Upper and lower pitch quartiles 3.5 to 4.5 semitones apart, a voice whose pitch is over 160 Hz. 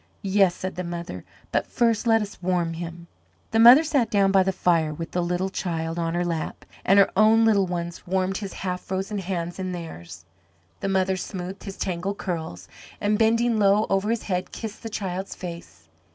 No: average, 2.9 semitones; high, 190 Hz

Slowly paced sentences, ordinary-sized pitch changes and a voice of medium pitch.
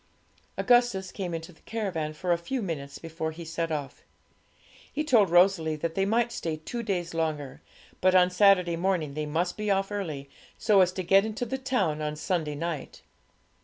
No: average, 185 wpm; average, 3.8 semitones; medium, 175 Hz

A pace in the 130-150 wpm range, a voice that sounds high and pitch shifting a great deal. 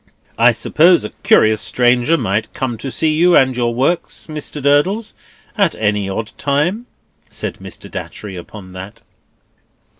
No: average, 145 wpm; low, 130 Hz; wide, 6.7 semitones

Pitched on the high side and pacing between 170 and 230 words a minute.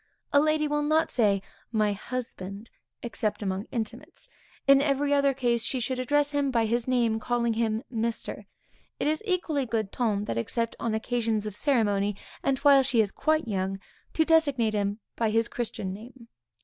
Yes: high, 235 Hz; average, 175 wpm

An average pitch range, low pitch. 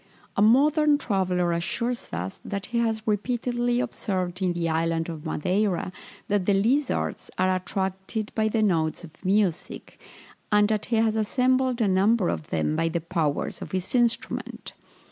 No: average, 4.8 semitones; high, 200 Hz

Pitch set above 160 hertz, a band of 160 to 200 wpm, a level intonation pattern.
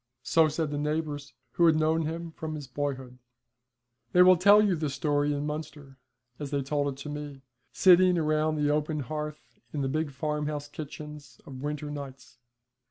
No: medium, 150 Hz; average, 175 wpm; narrow, 1.5 semitones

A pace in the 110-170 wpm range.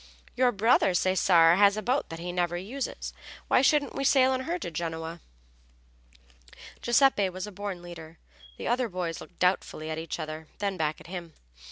No: average, 180 wpm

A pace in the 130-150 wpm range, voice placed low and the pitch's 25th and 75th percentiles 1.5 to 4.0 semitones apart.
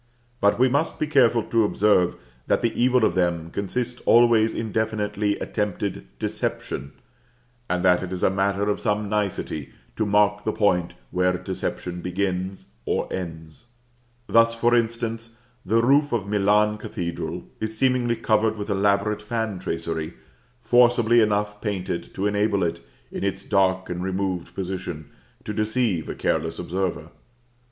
Yes: average, 145 wpm; low, 105 Hz; average, 3.6 semitones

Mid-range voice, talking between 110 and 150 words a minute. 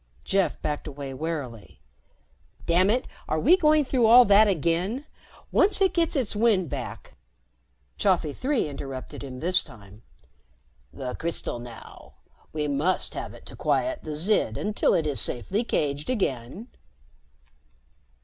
Yes: medium, 170 Hz; average, 140 wpm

